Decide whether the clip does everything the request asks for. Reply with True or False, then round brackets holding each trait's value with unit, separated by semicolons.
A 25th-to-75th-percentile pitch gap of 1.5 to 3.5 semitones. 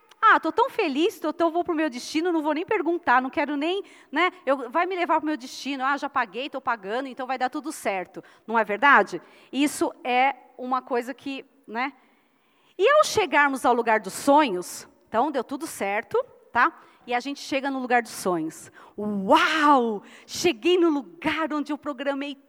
False (4.5 semitones)